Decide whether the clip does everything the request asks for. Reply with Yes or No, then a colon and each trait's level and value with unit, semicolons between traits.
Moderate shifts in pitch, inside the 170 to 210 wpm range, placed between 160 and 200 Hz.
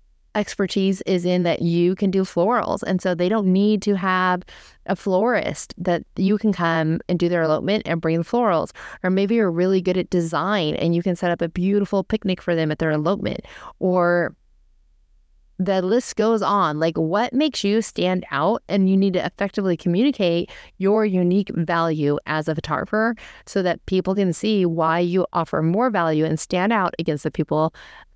Yes: average, 3.1 semitones; average, 190 wpm; medium, 185 Hz